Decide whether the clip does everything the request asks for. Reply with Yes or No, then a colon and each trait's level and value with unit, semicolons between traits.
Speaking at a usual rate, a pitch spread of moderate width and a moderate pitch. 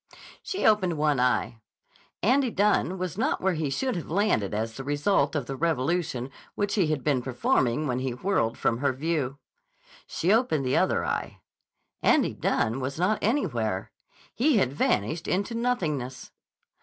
No: average, 160 wpm; wide, 7.4 semitones; medium, 150 Hz